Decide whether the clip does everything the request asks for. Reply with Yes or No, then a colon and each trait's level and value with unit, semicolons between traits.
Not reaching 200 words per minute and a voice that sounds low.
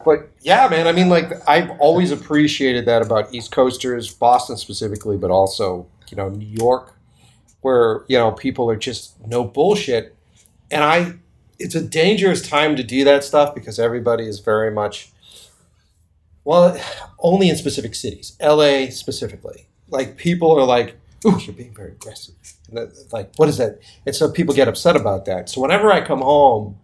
Yes: average, 170 wpm; low, 125 Hz